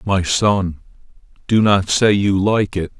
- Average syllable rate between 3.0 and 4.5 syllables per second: Yes, 3.7 syllables/s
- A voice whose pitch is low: Yes, low, 100 Hz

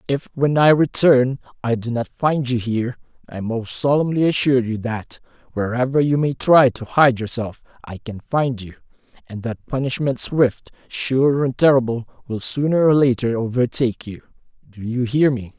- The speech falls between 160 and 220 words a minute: Yes, average, 170 wpm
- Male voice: Yes, male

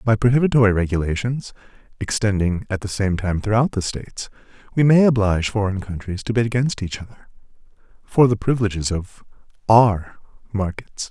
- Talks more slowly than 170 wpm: Yes, average, 145 wpm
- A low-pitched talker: Yes, low, 105 Hz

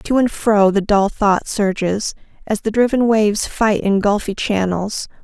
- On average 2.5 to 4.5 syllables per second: Yes, 4.2 syllables/s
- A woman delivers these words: Yes, female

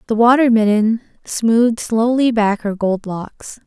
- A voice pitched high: Yes, high, 225 Hz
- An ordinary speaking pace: Yes, average, 145 wpm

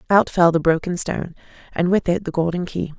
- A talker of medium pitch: Yes, medium, 175 Hz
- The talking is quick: Yes, fast, 220 wpm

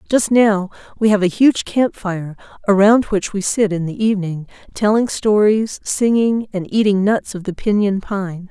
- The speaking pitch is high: Yes, high, 205 Hz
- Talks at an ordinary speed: Yes, average, 175 wpm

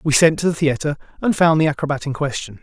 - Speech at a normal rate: No, fast, 250 wpm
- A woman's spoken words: No, male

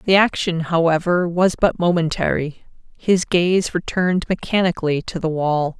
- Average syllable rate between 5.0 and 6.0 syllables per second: No, 4.7 syllables/s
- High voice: No, medium, 170 Hz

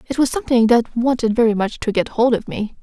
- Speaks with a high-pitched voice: Yes, high, 235 Hz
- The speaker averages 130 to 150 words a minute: No, fast, 255 wpm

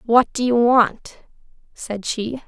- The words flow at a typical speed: Yes, average, 145 wpm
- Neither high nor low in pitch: No, high, 235 Hz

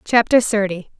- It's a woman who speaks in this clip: Yes, female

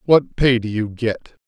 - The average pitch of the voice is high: No, low, 120 Hz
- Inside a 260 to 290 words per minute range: No, fast, 205 wpm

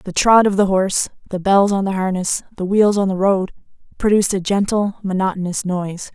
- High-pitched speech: Yes, high, 195 Hz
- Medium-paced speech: Yes, average, 195 wpm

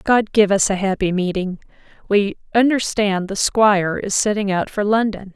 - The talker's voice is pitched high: Yes, high, 200 Hz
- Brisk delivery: No, average, 170 wpm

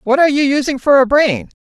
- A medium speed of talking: No, fast, 255 wpm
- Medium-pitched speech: No, very high, 270 Hz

